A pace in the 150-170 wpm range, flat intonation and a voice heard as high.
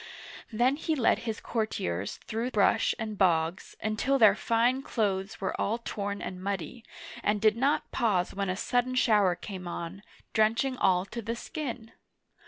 No: average, 160 wpm; average, 3.5 semitones; high, 215 Hz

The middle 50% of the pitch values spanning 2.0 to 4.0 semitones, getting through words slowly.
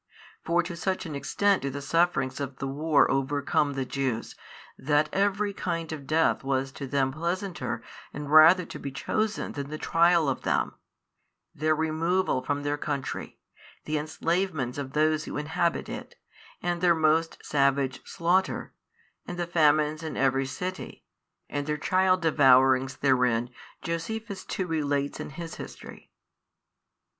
No: average, 3.7 semitones; average, 150 wpm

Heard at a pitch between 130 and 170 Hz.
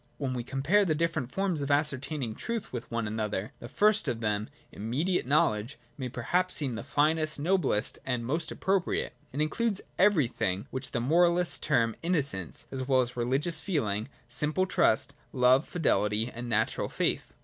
Yes: low, 135 Hz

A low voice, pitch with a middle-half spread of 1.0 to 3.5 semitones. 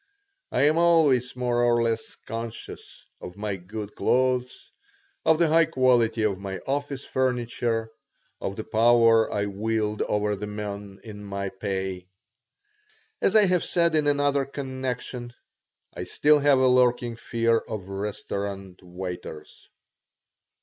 No: low, 115 Hz; average, 4.3 semitones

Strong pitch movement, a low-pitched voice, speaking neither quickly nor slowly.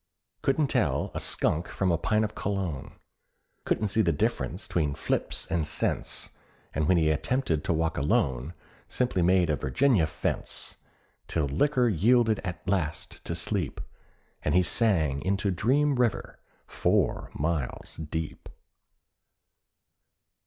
No: wide, 5.8 semitones; very low, 90 Hz; slow, 130 wpm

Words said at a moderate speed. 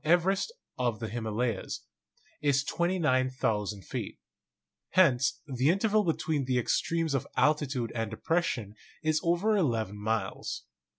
No: slow, 125 wpm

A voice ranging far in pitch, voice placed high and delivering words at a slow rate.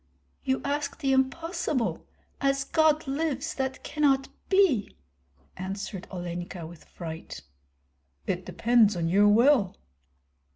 Yes: wide, 7.0 semitones; very high, 265 Hz; slow, 110 wpm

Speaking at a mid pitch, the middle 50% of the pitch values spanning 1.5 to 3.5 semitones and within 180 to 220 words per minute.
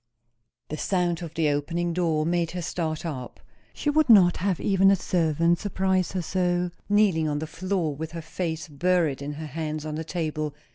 Yes: medium, 170 Hz; average, 2.8 semitones; average, 190 wpm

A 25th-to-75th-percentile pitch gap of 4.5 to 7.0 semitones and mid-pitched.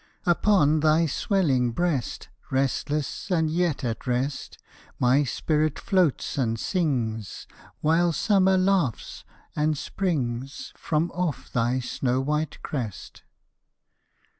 Yes: average, 5.2 semitones; medium, 150 Hz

